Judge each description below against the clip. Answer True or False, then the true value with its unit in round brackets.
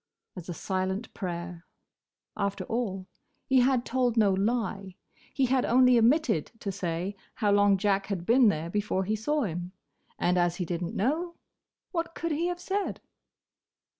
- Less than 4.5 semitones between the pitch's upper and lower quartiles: False (5.2 semitones)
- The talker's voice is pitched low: False (205 Hz)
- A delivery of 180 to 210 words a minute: False (165 wpm)